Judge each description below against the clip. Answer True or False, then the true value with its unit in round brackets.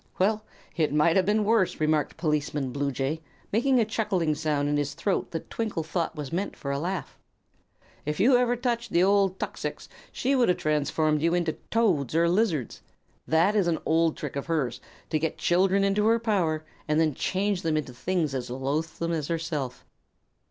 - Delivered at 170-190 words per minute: True (185 wpm)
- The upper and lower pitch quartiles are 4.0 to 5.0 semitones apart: True (4.7 semitones)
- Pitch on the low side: False (165 Hz)